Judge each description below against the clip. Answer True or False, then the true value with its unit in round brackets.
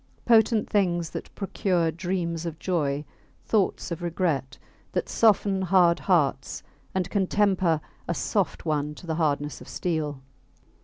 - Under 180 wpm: True (140 wpm)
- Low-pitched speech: False (170 Hz)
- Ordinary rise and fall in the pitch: True (3.6 semitones)